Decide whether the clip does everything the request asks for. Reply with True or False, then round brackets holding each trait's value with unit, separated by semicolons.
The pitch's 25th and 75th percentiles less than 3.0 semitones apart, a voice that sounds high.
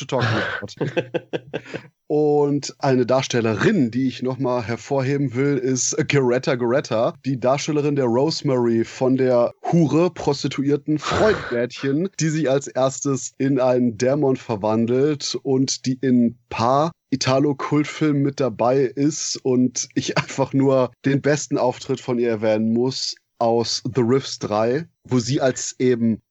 False (2.5 semitones; 130 Hz)